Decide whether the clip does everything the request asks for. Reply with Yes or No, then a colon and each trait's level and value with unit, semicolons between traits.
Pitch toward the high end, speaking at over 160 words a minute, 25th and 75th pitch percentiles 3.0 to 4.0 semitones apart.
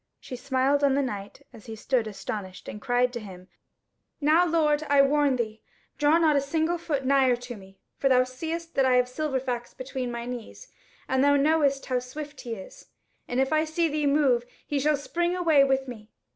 Yes: very high, 270 Hz; average, 200 wpm; average, 3.4 semitones